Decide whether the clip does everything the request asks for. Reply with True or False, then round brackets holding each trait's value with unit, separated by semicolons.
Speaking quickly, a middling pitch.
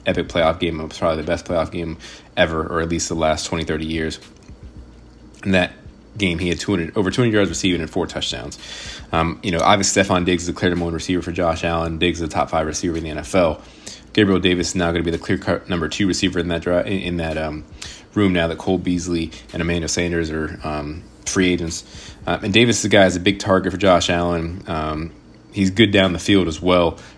False (230 wpm; 85 Hz)